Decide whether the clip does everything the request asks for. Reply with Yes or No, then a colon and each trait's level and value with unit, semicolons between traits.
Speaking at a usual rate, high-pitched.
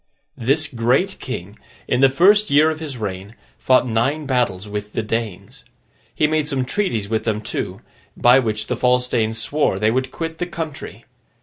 No: average, 180 wpm; low, 125 Hz